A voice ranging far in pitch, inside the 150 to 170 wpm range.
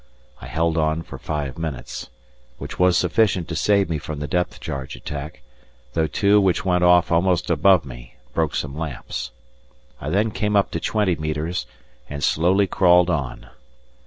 No: average, 3.3 semitones; average, 165 wpm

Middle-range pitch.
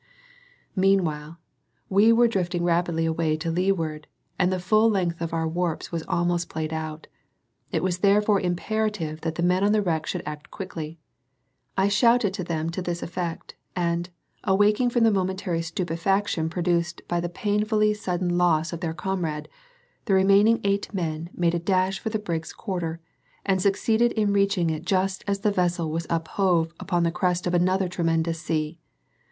Yes: medium, 175 Hz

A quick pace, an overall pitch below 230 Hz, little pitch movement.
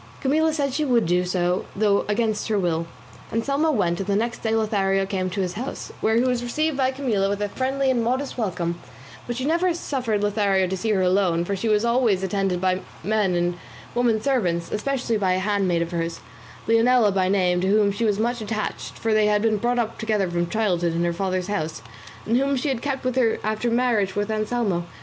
No: fast, 225 wpm; high, 210 Hz; average, 4.4 semitones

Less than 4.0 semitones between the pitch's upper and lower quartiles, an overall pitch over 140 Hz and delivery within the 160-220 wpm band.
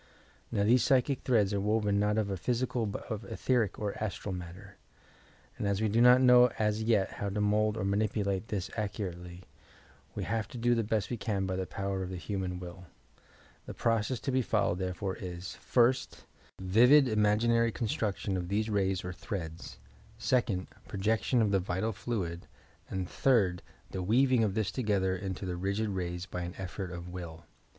No: average, 3.3 semitones; low, 100 Hz; average, 180 wpm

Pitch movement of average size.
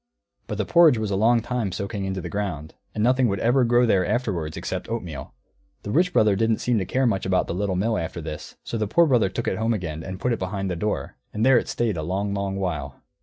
Yes: average, 4.0 semitones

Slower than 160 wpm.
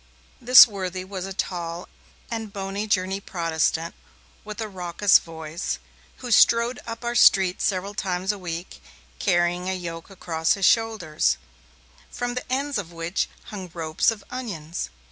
Yes: average, 145 wpm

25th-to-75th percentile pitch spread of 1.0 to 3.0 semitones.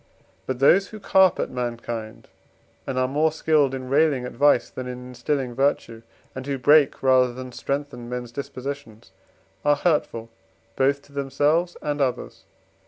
Yes: average, 2.7 semitones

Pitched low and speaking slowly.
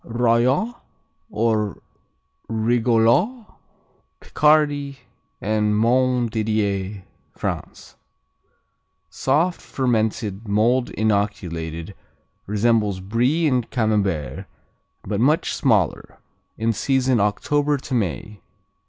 Yes: low, 115 Hz; slow, 75 wpm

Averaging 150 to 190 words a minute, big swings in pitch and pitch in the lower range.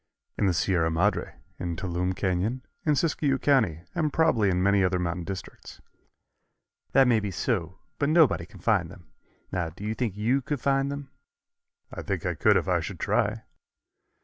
Yes: average, 175 wpm; wide, 7.1 semitones; low, 100 Hz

